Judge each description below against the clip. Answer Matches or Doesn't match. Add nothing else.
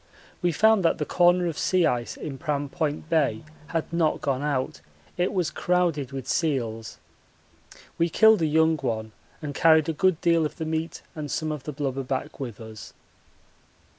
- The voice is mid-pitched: Matches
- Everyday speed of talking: Matches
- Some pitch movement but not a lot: Matches